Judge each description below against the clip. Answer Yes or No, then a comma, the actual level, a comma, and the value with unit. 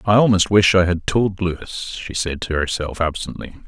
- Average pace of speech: Yes, average, 195 wpm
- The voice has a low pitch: Yes, very low, 90 Hz